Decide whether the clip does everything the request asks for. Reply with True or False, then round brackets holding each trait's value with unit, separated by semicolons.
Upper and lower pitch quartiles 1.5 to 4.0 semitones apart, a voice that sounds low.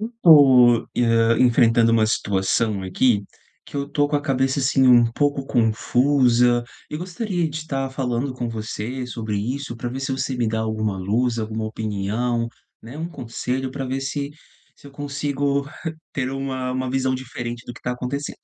True (3.2 semitones; 125 Hz)